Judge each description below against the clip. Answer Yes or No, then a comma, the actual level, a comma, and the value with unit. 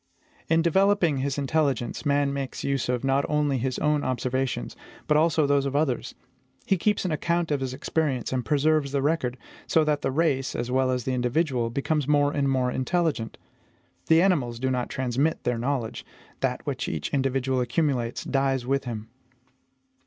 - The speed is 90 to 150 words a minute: No, average, 175 wpm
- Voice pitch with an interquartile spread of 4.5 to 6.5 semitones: No, average, 3.0 semitones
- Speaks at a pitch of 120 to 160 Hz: Yes, low, 135 Hz